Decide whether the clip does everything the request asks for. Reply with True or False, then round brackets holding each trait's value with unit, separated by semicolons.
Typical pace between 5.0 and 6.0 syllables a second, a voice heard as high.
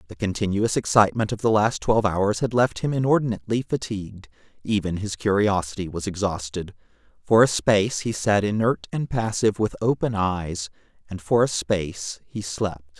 False (5.3 syllables/s; 100 Hz)